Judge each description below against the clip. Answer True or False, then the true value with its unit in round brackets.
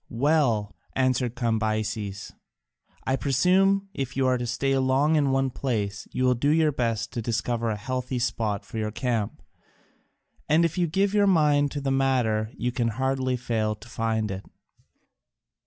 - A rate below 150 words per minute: False (165 wpm)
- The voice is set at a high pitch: False (125 Hz)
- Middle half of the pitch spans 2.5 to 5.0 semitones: True (3.8 semitones)